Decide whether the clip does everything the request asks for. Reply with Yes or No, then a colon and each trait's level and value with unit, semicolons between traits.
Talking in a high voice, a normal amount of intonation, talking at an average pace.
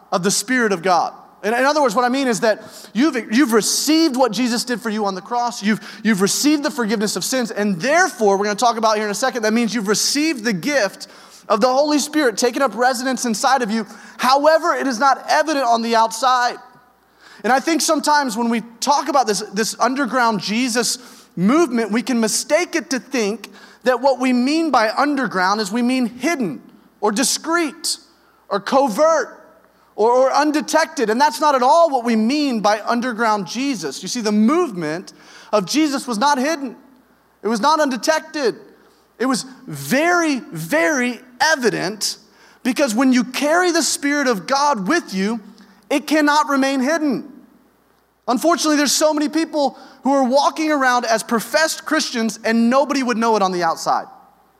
Yes: very high, 255 Hz; average, 4.6 semitones; average, 180 wpm